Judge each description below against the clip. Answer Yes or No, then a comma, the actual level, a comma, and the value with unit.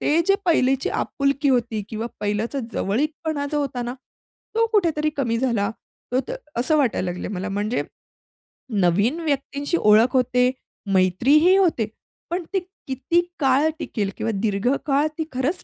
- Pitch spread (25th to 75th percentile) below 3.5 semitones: No, wide, 5.5 semitones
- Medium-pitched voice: No, very high, 260 Hz